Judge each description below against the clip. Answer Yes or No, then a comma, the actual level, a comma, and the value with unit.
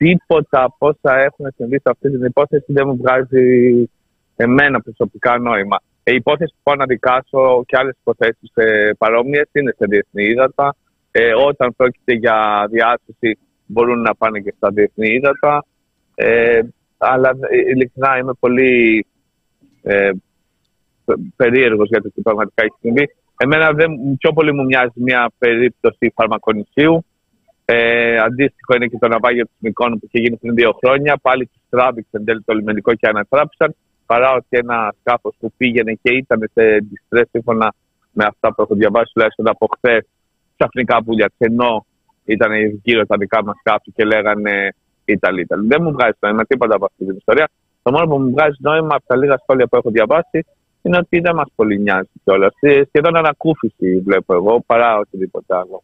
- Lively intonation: No, average, 4.0 semitones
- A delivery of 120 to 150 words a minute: No, average, 160 wpm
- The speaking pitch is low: Yes, low, 120 Hz